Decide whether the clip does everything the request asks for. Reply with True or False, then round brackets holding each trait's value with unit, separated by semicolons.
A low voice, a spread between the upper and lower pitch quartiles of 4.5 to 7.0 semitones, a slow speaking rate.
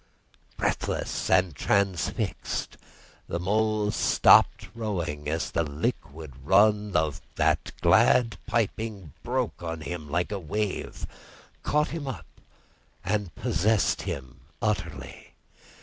True (95 Hz; 5.1 semitones; 105 wpm)